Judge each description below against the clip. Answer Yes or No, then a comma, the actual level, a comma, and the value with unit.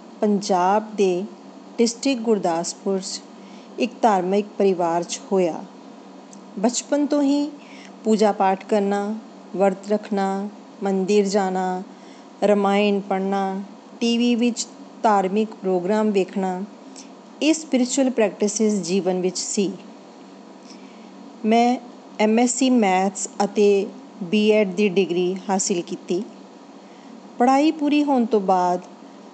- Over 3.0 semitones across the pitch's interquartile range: Yes, average, 3.7 semitones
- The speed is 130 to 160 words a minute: No, slow, 95 wpm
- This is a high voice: Yes, high, 210 Hz